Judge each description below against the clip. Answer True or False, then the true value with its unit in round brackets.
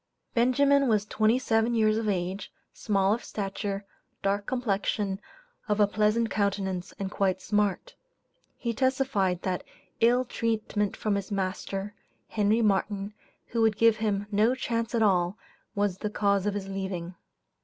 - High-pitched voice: True (205 Hz)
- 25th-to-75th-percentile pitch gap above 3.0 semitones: False (2.5 semitones)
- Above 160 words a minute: False (145 wpm)